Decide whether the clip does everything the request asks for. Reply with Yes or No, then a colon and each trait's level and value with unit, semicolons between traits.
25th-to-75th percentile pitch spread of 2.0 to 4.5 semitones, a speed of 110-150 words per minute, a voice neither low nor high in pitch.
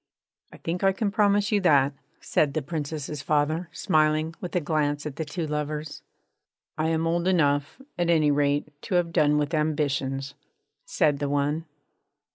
No: narrow, 2.5 semitones; average, 165 wpm; medium, 155 Hz